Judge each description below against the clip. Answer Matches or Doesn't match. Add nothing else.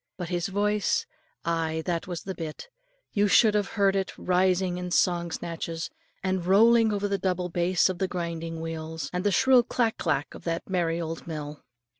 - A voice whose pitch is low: Doesn't match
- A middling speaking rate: Matches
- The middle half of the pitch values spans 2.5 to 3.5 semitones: Matches